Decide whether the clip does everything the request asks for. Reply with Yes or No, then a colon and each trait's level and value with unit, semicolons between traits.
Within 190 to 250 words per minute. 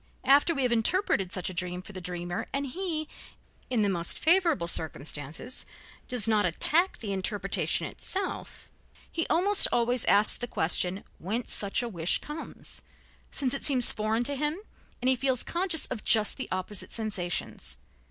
No: average, 160 wpm